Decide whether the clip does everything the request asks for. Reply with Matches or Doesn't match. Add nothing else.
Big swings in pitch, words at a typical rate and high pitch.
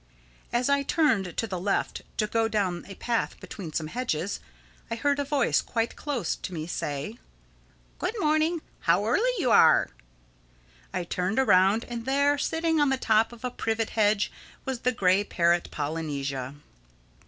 Matches